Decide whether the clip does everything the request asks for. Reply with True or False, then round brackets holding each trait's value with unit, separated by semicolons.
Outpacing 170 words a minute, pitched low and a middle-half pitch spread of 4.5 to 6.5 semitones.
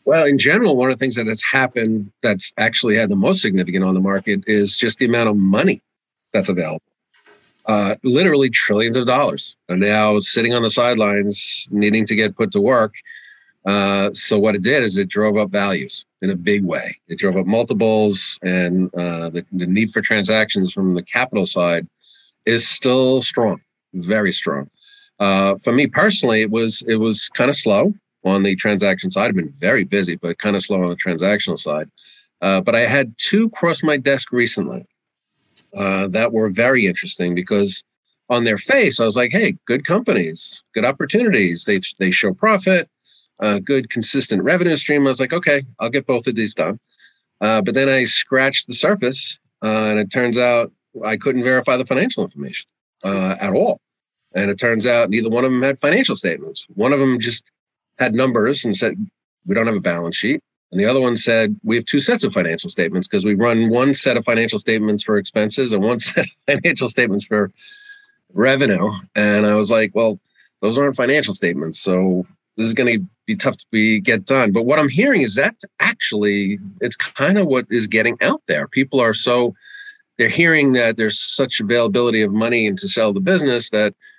True (200 wpm; 115 Hz; 4.9 semitones)